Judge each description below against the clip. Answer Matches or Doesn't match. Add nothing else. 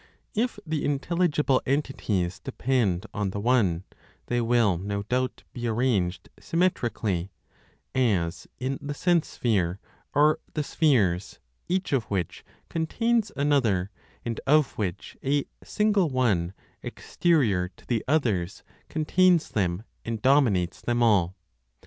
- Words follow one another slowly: Matches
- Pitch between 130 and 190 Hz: Doesn't match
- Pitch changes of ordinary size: Doesn't match